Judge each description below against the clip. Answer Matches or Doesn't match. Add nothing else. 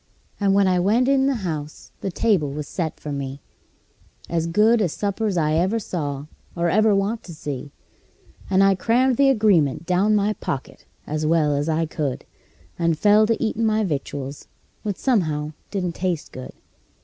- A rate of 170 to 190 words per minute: Matches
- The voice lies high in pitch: Doesn't match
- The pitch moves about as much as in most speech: Doesn't match